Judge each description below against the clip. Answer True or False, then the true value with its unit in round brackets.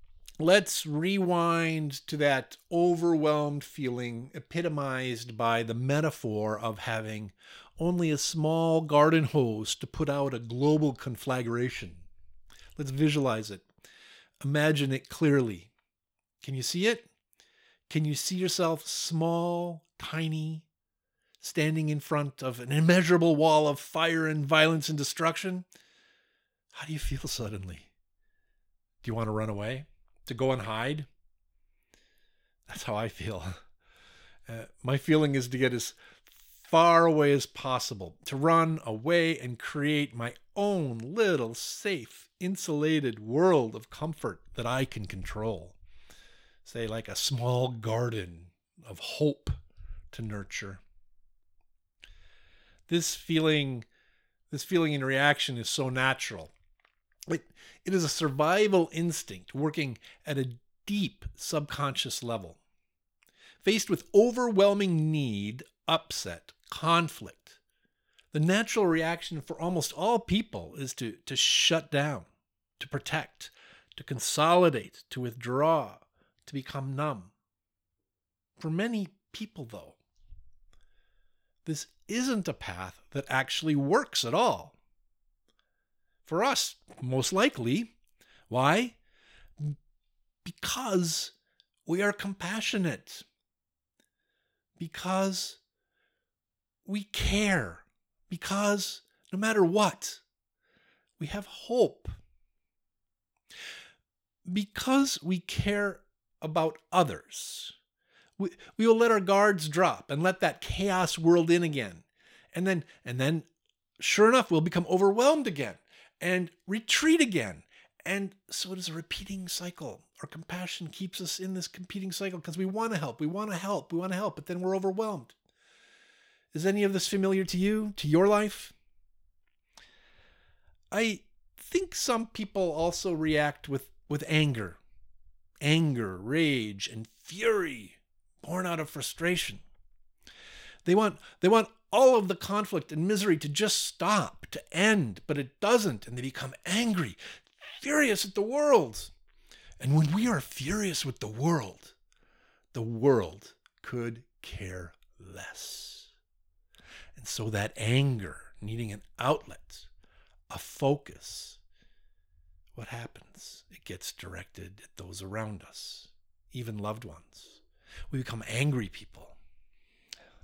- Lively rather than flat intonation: True (8.2 semitones)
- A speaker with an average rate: False (120 wpm)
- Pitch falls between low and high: True (150 Hz)